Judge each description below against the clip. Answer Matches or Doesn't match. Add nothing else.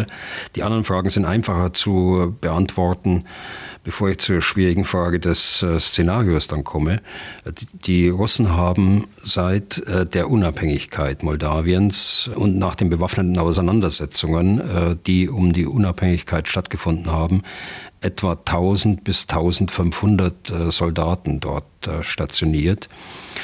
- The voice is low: Matches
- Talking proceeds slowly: Matches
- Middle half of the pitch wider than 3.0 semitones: Doesn't match